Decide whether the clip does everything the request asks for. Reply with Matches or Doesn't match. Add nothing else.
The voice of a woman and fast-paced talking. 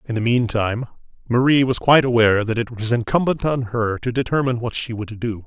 Doesn't match